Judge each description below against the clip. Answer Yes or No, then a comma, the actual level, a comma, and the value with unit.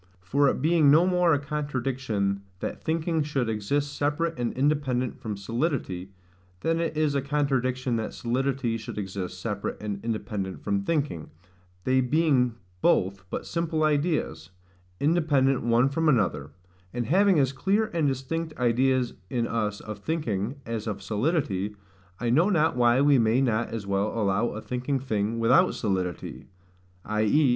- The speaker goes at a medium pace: Yes, average, 150 wpm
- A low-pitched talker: Yes, low, 130 Hz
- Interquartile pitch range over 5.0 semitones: Yes, wide, 5.6 semitones